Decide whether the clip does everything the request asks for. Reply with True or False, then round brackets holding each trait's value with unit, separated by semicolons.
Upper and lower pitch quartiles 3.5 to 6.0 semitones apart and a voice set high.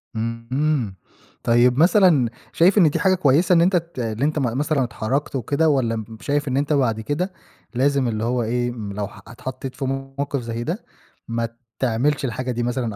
False (4.2 semitones; 130 Hz)